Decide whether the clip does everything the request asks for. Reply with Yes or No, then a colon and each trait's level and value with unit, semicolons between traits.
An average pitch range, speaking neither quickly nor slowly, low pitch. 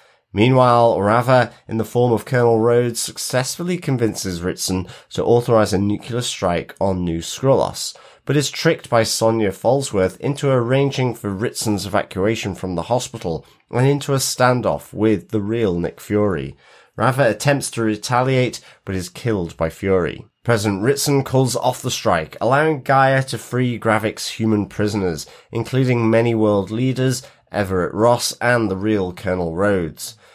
Yes: average, 3.8 semitones; average, 150 wpm; low, 115 Hz